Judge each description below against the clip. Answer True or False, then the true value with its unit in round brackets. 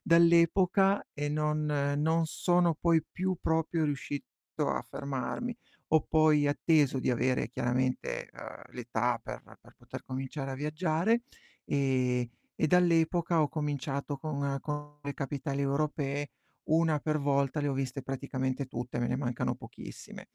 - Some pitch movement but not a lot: True (3.1 semitones)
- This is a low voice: False (145 Hz)